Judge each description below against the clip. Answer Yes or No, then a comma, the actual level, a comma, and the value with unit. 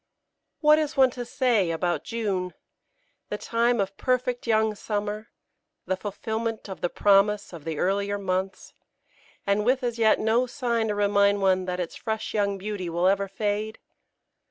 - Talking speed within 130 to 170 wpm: Yes, average, 160 wpm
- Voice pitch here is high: Yes, high, 205 Hz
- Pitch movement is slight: No, average, 3.0 semitones